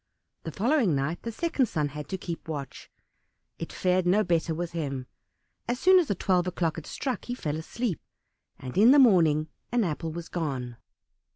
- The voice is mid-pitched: Yes, medium, 170 Hz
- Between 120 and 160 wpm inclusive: No, average, 180 wpm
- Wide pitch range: Yes, wide, 6.4 semitones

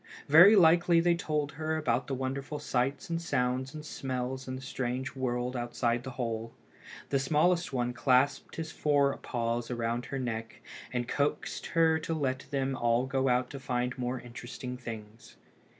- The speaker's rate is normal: Yes, average, 165 wpm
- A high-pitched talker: No, low, 130 Hz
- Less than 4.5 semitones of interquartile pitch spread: Yes, average, 3.1 semitones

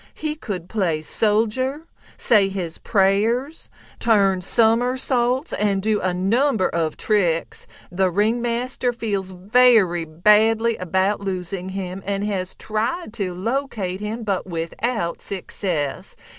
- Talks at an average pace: No, slow, 115 wpm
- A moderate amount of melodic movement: Yes, average, 4.1 semitones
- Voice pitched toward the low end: No, high, 205 Hz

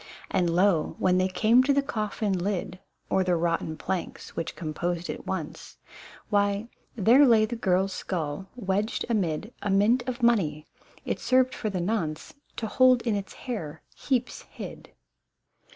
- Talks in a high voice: Yes, high, 200 Hz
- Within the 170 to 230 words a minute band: No, average, 150 wpm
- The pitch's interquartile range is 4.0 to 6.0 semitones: Yes, average, 4.7 semitones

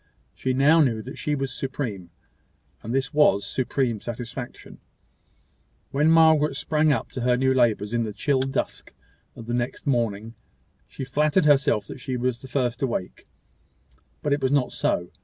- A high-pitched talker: No, low, 130 Hz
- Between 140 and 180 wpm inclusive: Yes, average, 165 wpm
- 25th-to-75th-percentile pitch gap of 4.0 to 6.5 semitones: No, average, 3.4 semitones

